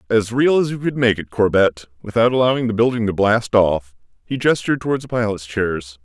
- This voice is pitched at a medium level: No, low, 110 Hz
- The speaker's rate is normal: No, fast, 210 wpm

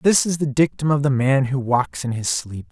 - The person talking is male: Yes, male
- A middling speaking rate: No, fast, 265 wpm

